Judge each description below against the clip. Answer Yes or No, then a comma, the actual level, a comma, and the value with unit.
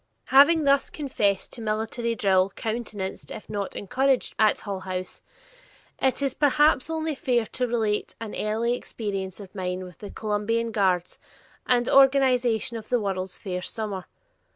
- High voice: Yes, high, 220 Hz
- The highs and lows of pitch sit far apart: No, average, 4.3 semitones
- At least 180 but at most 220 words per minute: No, average, 150 wpm